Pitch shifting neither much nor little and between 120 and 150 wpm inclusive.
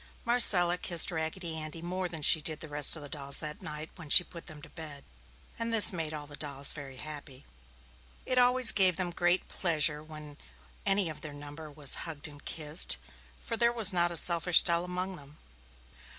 No: average, 3.2 semitones; average, 195 wpm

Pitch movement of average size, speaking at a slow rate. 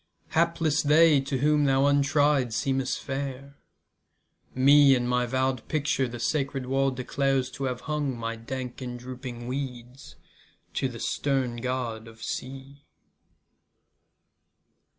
No: narrow, 2.3 semitones; slow, 125 wpm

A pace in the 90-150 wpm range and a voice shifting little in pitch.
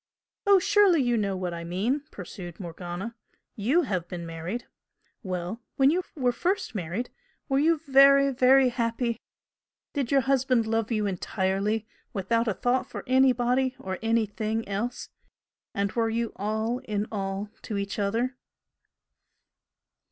No: average, 140 wpm; average, 4.6 semitones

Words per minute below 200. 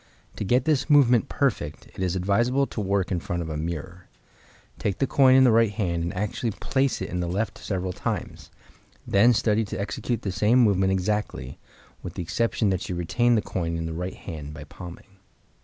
No: fast, 205 wpm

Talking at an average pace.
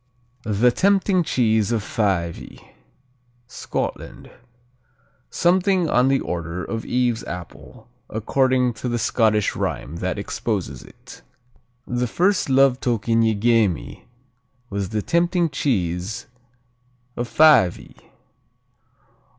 No: slow, 105 wpm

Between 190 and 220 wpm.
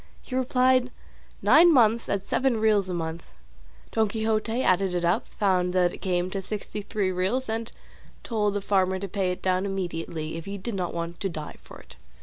Yes: average, 195 wpm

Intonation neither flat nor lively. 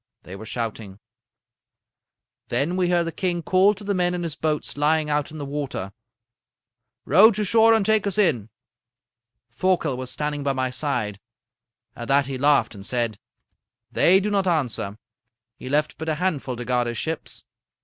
No: wide, 6.3 semitones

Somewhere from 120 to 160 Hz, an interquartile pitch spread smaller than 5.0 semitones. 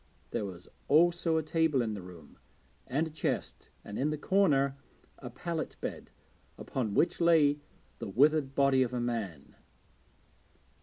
No: medium, 140 Hz; wide, 5.4 semitones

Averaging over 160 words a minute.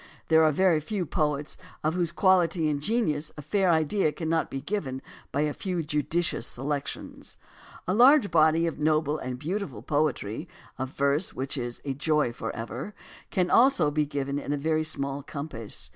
Yes: average, 170 wpm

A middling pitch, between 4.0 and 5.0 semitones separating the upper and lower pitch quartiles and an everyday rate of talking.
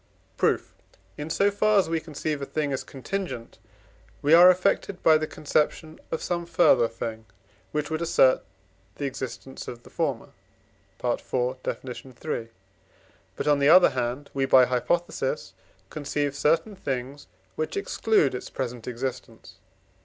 Yes: medium, 145 Hz; average, 4.4 semitones; average, 145 wpm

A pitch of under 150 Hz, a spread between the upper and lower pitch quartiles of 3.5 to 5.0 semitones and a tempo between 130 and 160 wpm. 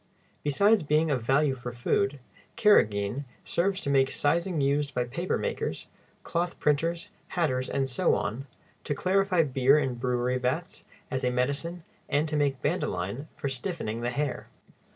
Yes: medium, 140 Hz; average, 4.7 semitones; average, 155 wpm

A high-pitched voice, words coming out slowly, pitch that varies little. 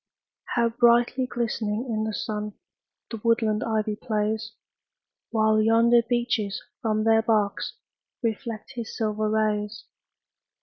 Yes: high, 220 Hz; slow, 115 wpm; narrow, 1.5 semitones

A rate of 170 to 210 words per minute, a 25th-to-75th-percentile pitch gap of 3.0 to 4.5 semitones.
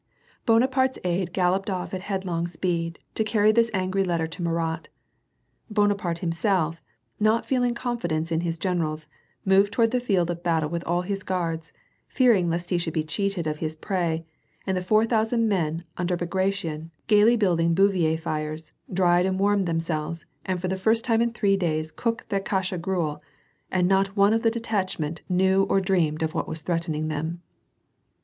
Yes: average, 180 wpm; average, 3.4 semitones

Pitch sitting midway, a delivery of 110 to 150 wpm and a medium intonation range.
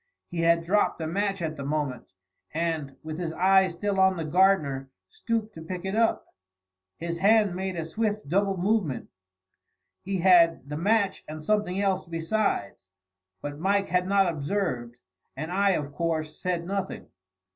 No: medium, 180 Hz; average, 160 wpm; average, 3.8 semitones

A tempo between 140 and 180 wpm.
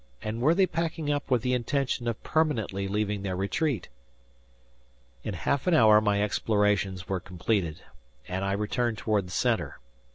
Yes: average, 160 wpm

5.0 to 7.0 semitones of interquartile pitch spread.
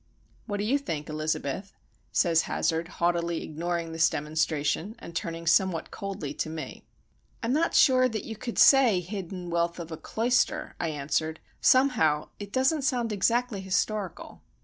Yes: wide, 5.6 semitones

